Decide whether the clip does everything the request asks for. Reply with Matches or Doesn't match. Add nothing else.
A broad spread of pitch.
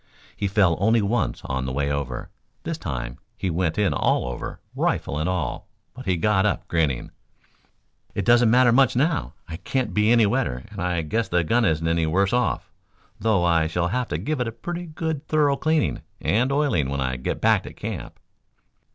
Matches